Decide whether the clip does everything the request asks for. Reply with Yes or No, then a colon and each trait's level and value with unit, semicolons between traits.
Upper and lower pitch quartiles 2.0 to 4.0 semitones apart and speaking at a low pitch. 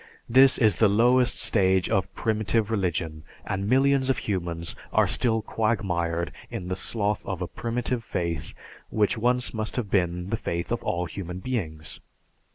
No: average, 4.8 semitones; low, 100 Hz